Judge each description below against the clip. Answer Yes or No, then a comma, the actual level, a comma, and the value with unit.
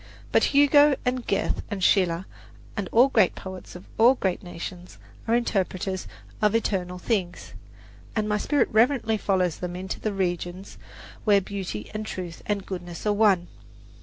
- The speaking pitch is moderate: No, high, 195 Hz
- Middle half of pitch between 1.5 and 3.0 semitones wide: No, average, 3.4 semitones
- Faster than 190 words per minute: No, average, 155 wpm